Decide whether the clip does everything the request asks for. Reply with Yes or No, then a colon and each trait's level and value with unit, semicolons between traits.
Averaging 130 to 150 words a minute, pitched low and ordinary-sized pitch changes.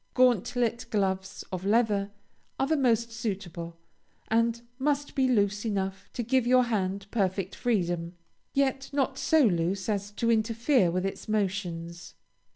No: average, 140 wpm; high, 215 Hz; average, 4.2 semitones